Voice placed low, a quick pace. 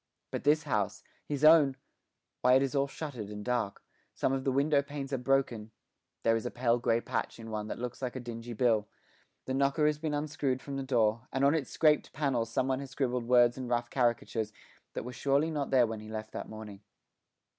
Yes: low, 125 Hz; fast, 215 wpm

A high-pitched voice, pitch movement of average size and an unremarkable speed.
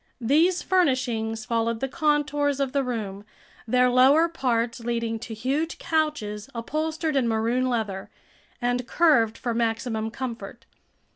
No: very high, 250 Hz; average, 4.3 semitones; slow, 130 wpm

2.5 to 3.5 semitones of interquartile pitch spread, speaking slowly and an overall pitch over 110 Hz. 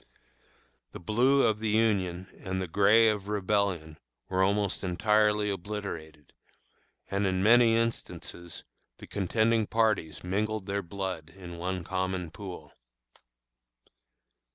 No: average, 2.9 semitones; slow, 115 wpm; low, 100 Hz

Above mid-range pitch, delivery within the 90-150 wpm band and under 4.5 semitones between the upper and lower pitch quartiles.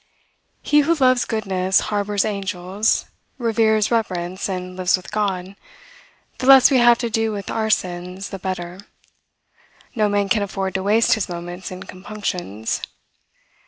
Yes: high, 200 Hz; average, 145 wpm; average, 3.1 semitones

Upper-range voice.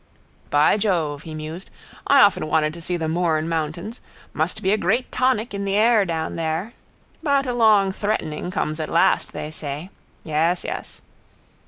No: medium, 175 Hz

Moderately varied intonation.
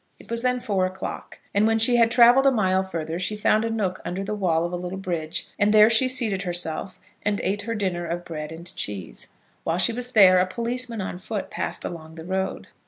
Yes: average, 4.3 semitones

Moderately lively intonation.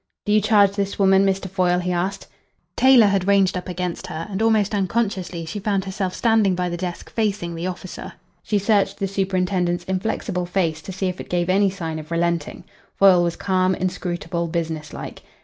No: narrow, 2.3 semitones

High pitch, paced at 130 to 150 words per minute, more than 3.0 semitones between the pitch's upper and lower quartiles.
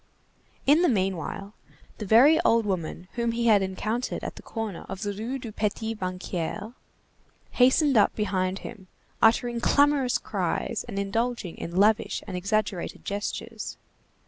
Yes: high, 215 Hz; average, 145 wpm; average, 3.6 semitones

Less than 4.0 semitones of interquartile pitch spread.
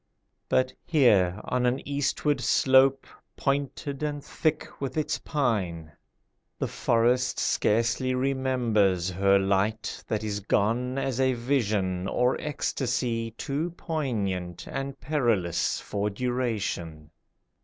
No: average, 5.3 semitones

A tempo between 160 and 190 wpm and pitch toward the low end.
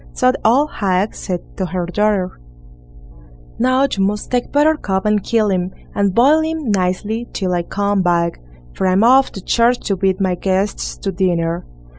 No: average, 175 wpm; high, 195 Hz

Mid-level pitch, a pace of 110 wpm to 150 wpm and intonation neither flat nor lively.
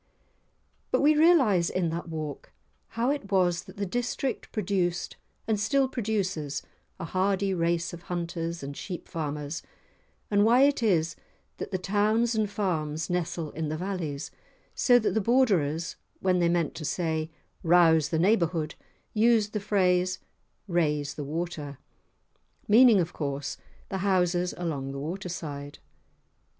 Yes: medium, 180 Hz; average, 140 wpm; average, 4.3 semitones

